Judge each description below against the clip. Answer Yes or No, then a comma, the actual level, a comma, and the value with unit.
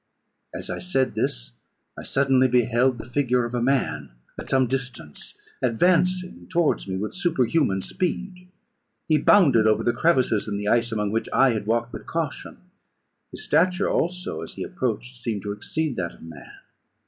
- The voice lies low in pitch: Yes, low, 125 Hz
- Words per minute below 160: No, average, 170 wpm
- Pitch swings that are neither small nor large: No, wide, 6.9 semitones